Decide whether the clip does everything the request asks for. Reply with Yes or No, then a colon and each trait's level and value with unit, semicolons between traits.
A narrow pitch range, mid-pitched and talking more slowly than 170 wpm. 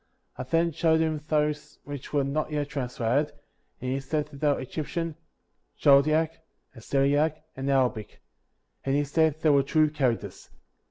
Yes: narrow, 2.2 semitones; medium, 145 Hz; average, 155 wpm